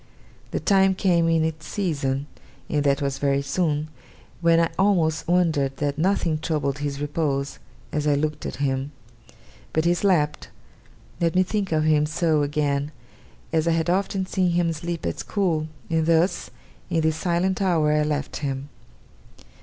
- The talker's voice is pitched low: No, medium, 160 Hz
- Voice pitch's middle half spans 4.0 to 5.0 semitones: No, average, 2.9 semitones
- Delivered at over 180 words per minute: No, average, 160 wpm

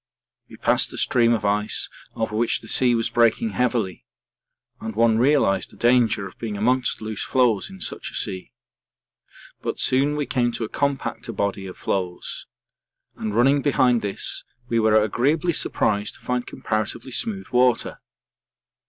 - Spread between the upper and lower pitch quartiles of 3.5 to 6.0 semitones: No, average, 3.1 semitones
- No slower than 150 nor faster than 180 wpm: Yes, average, 160 wpm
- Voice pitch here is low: Yes, low, 115 Hz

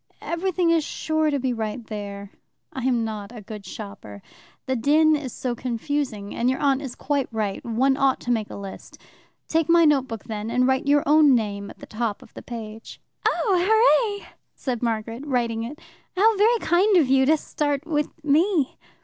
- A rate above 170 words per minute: Yes, average, 185 wpm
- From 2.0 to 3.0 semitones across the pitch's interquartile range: No, wide, 5.4 semitones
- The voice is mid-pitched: No, very high, 260 Hz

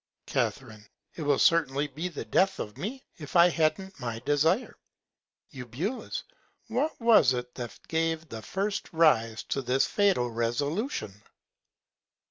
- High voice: No, medium, 155 Hz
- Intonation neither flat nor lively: No, wide, 7.4 semitones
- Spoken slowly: Yes, slow, 130 wpm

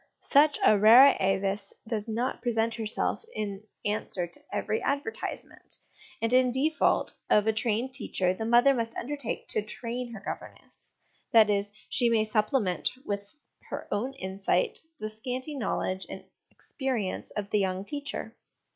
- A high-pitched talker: Yes, high, 220 Hz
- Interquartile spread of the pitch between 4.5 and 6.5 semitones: No, average, 3.7 semitones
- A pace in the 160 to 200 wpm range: No, average, 145 wpm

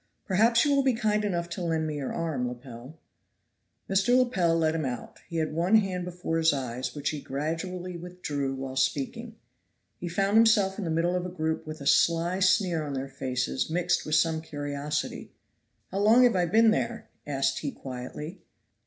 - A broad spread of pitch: No, average, 4.9 semitones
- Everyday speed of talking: Yes, average, 190 wpm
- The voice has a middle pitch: Yes, medium, 165 Hz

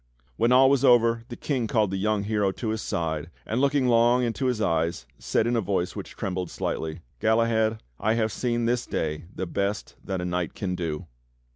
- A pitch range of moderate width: Yes, average, 4.6 semitones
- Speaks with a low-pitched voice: Yes, low, 110 Hz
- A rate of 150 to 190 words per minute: No, fast, 205 wpm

